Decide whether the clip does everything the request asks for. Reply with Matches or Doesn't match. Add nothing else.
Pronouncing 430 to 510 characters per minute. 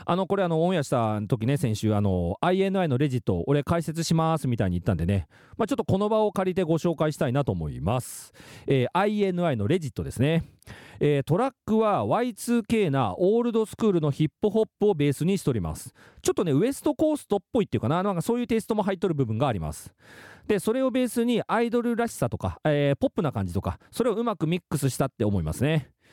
Matches